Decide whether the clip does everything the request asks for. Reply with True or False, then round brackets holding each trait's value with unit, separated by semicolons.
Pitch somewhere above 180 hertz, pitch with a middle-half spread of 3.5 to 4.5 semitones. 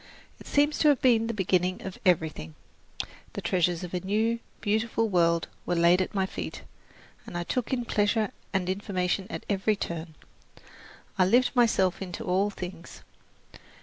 True (190 Hz; 3.9 semitones)